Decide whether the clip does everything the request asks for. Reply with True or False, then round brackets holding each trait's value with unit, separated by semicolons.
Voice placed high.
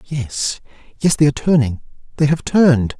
False (140 Hz)